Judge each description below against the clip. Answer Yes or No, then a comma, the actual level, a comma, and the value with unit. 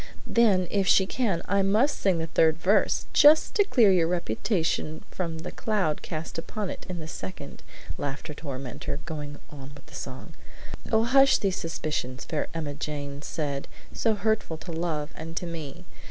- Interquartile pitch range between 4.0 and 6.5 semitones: Yes, average, 5.0 semitones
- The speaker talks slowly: No, average, 170 wpm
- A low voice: No, medium, 165 Hz